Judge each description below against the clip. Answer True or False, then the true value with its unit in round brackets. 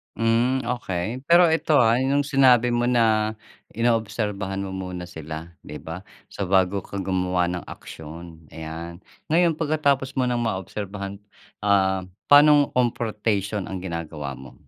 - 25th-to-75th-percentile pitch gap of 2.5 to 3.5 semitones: False (5.3 semitones)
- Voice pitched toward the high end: False (100 Hz)